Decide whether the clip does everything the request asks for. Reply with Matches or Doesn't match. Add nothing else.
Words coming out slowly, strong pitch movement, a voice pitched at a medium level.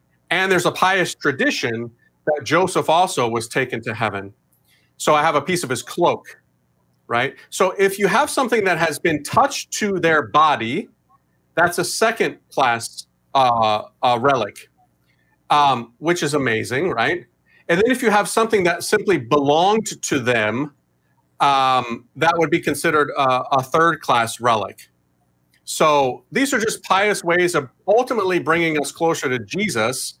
Doesn't match